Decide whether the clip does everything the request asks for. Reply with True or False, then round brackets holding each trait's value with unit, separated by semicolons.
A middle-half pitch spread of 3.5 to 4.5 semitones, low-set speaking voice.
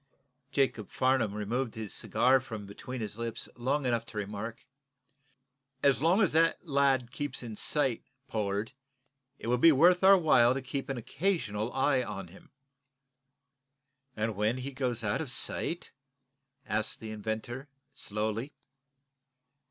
True (4.0 semitones; 120 Hz)